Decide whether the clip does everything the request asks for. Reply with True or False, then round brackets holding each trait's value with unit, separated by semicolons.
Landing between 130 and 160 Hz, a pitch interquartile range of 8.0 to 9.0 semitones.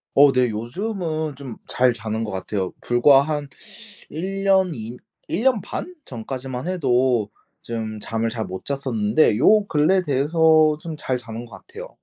False (135 Hz; 5.6 semitones)